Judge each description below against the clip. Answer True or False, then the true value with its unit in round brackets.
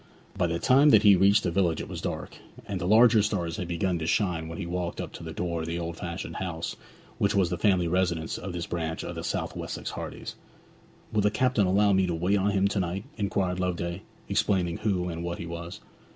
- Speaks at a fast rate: True (235 wpm)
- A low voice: True (90 Hz)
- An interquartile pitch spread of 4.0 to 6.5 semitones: False (2.8 semitones)